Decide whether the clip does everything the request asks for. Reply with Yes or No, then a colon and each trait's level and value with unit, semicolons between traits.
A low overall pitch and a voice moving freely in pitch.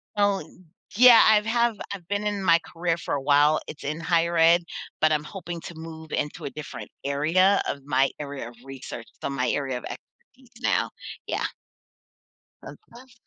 No: medium, 165 Hz; wide, 5.8 semitones